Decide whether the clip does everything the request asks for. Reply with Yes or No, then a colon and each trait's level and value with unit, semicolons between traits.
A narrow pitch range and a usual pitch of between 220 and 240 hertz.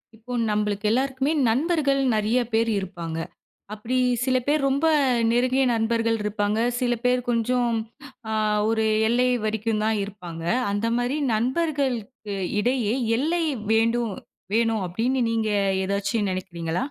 No: average, 3.3 semitones; high, 230 Hz